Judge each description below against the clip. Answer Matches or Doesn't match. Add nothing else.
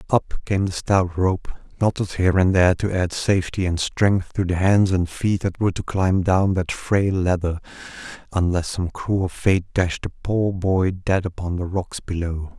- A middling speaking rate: Matches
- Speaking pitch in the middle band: Doesn't match